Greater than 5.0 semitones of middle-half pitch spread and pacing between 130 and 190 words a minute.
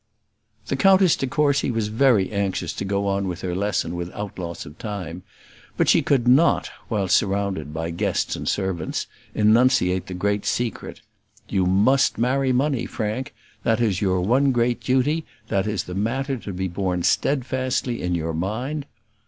Yes: wide, 5.6 semitones; average, 165 wpm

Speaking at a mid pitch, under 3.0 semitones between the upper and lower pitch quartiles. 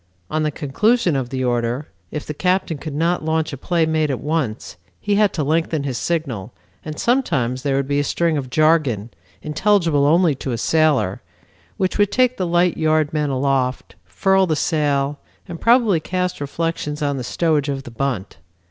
No: medium, 150 Hz; average, 3.7 semitones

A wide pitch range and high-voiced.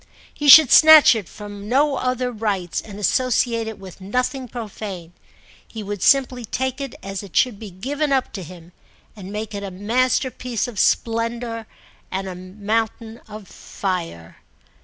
No: average, 4.3 semitones; high, 220 Hz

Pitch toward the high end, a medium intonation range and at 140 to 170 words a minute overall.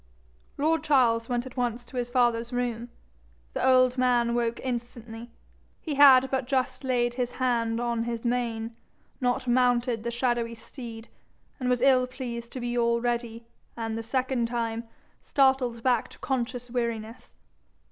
No: high, 240 Hz; narrow, 1.5 semitones; average, 150 wpm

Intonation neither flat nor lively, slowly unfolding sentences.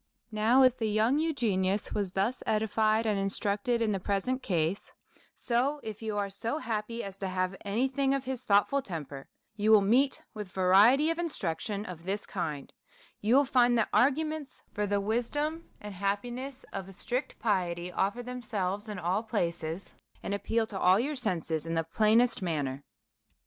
No: average, 4.3 semitones; average, 175 wpm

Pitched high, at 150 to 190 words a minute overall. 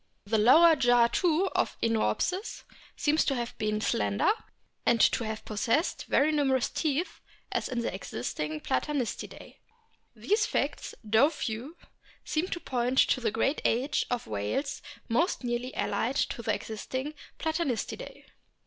No: very high, 250 Hz; average, 140 wpm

